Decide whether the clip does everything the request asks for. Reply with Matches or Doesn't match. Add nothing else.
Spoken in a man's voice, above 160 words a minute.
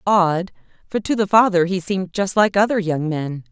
Doesn't match